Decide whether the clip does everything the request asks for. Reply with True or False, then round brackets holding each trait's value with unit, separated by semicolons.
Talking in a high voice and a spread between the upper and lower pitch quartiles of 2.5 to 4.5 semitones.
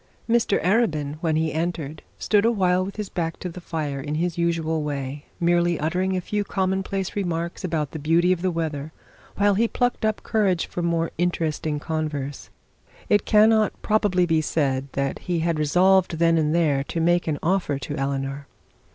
False (170 Hz; 3.5 semitones)